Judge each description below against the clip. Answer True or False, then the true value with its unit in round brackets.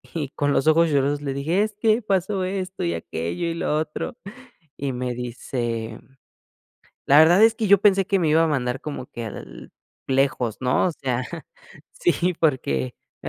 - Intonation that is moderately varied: False (6.6 semitones)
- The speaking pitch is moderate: True (145 Hz)